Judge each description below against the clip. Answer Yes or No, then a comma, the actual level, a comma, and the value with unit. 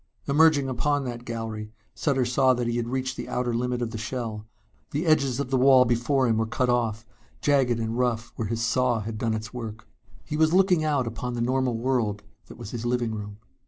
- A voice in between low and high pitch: No, low, 120 Hz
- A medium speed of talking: No, fast, 215 wpm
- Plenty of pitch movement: No, narrow, 2.6 semitones